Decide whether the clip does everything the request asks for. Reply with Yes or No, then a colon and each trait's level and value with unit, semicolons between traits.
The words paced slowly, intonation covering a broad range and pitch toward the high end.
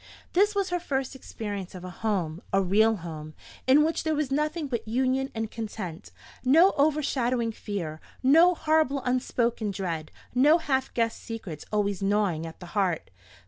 No: average, 160 wpm; wide, 6.6 semitones; high, 230 Hz